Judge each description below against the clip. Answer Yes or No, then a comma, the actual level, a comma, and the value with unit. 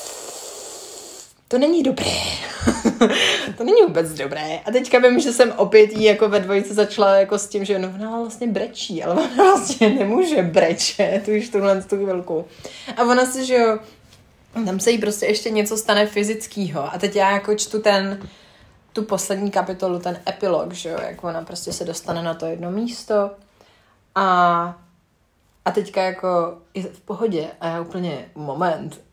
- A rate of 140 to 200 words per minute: Yes, fast, 170 wpm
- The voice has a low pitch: No, high, 200 Hz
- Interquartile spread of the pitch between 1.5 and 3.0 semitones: No, average, 4.1 semitones